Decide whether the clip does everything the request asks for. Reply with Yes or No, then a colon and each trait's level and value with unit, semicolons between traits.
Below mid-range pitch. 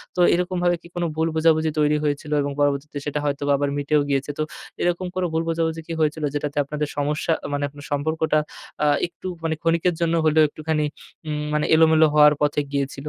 No: medium, 150 Hz